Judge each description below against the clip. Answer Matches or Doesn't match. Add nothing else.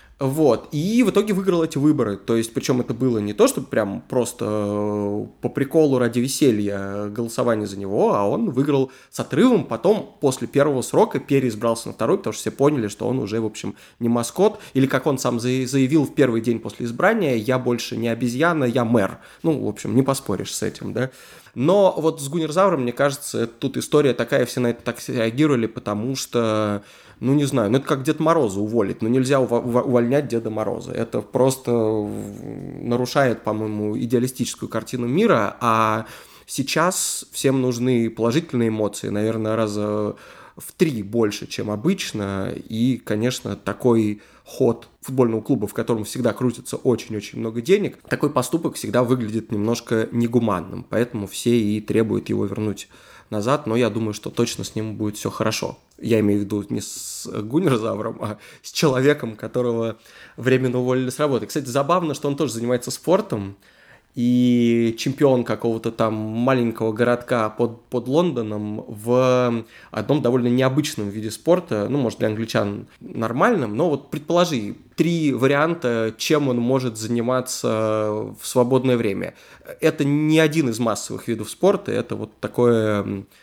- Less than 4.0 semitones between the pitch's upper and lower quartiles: Matches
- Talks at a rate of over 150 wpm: Matches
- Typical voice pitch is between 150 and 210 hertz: Doesn't match